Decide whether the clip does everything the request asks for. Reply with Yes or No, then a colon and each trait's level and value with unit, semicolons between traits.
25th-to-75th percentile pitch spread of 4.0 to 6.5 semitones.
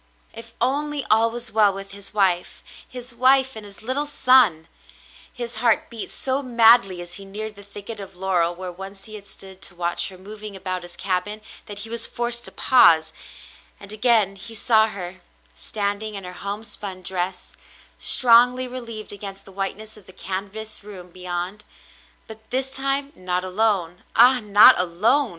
No: average, 3.6 semitones